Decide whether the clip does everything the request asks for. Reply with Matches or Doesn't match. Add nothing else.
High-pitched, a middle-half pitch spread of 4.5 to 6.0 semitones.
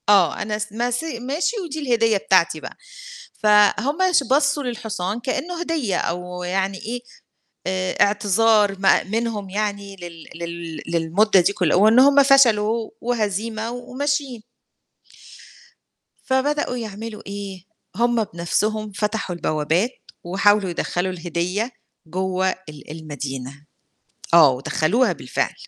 Matches